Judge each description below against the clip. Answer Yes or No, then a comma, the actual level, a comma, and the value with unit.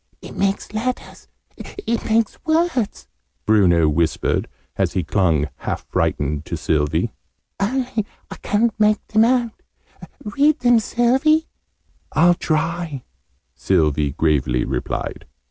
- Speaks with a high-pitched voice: Yes, high, 195 Hz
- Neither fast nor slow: No, slow, 110 wpm